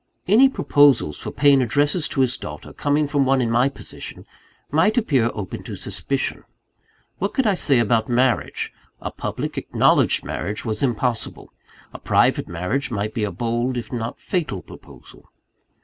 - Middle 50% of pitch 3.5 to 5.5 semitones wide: Yes, average, 4.1 semitones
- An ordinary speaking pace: Yes, average, 160 wpm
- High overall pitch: No, low, 130 Hz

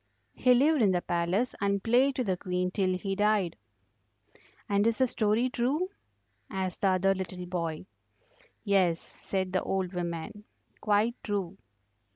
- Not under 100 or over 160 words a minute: Yes, average, 150 wpm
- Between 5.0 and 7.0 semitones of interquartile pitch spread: No, average, 3.5 semitones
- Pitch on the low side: No, high, 195 Hz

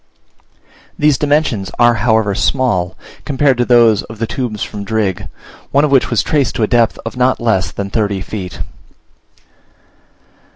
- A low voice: Yes, low, 115 Hz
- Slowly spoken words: No, average, 155 wpm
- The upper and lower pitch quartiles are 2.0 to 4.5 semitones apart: Yes, average, 4.0 semitones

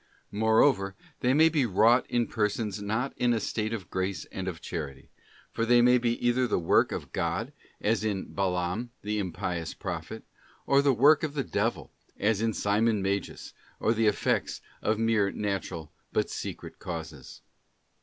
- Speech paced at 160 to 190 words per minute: Yes, average, 165 wpm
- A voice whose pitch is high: No, low, 110 Hz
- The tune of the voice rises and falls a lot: No, average, 3.6 semitones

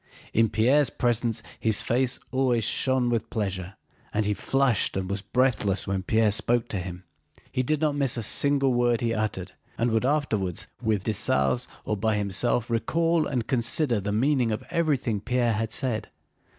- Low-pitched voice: Yes, low, 115 Hz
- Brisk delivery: No, average, 170 wpm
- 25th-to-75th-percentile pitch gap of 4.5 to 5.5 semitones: No, average, 3.6 semitones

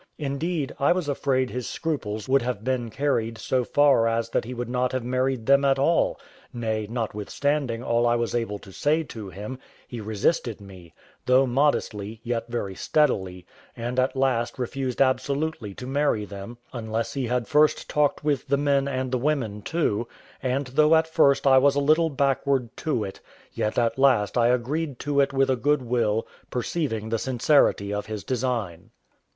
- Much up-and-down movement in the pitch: No, average, 3.5 semitones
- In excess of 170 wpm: Yes, average, 180 wpm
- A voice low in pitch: Yes, low, 125 Hz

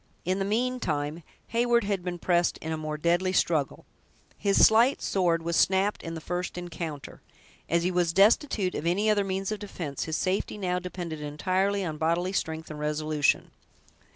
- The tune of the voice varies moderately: Yes, average, 3.5 semitones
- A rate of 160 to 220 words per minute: Yes, average, 175 wpm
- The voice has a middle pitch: Yes, medium, 180 Hz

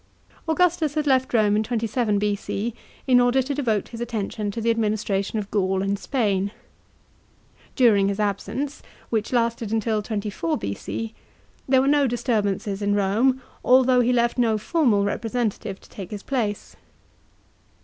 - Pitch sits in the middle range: No, high, 220 Hz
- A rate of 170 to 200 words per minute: No, average, 150 wpm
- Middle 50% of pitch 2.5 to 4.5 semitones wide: Yes, average, 3.5 semitones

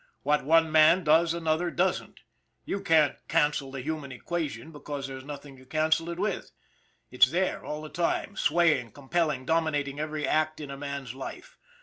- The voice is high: No, medium, 155 Hz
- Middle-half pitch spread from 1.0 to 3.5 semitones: Yes, average, 2.8 semitones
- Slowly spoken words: No, average, 165 wpm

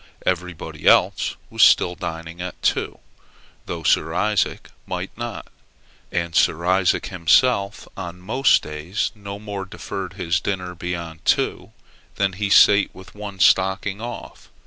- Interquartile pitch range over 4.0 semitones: No, average, 2.7 semitones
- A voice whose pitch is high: No, very low, 95 Hz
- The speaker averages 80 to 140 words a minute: Yes, slow, 135 wpm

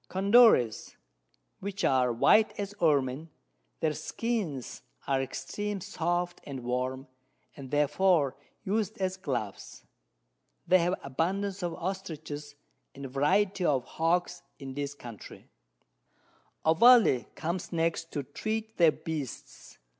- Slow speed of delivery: Yes, slow, 115 wpm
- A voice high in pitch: No, medium, 165 Hz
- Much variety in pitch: Yes, wide, 5.8 semitones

